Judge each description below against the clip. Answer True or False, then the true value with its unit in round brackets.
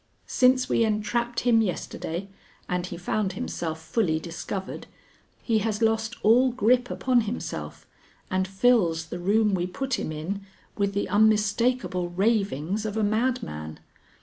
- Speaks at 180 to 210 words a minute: False (140 wpm)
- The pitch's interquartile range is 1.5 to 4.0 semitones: False (4.5 semitones)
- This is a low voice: False (210 Hz)